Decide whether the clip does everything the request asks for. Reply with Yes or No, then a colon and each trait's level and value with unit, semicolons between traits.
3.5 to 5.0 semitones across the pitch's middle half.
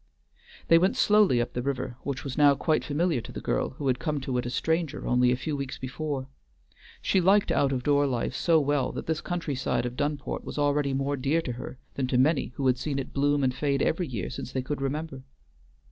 No: average, 2.8 semitones